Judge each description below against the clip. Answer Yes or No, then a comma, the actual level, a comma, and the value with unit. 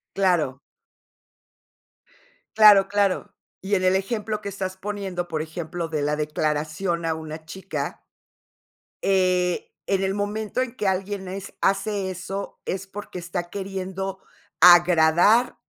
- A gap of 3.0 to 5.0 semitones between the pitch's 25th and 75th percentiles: No, narrow, 2.4 semitones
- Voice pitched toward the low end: No, high, 190 Hz